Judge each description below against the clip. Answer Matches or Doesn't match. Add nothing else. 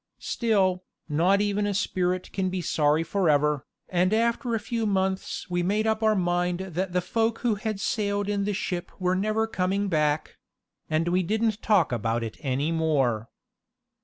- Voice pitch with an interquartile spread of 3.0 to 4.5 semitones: Matches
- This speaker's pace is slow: Doesn't match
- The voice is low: Doesn't match